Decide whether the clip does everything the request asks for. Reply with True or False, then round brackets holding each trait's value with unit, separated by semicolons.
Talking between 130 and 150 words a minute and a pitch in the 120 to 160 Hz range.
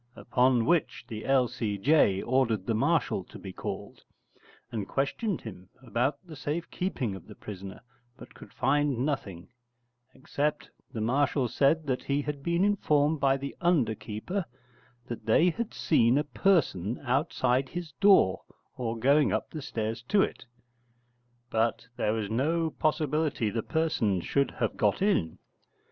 True (145 wpm; 135 Hz)